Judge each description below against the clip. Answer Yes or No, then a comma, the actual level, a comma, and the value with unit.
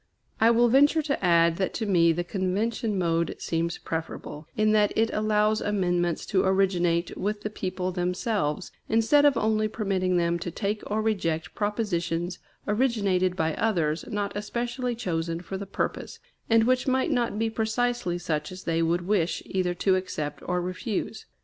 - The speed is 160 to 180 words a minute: Yes, average, 165 wpm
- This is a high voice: Yes, high, 195 Hz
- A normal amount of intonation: Yes, average, 4.1 semitones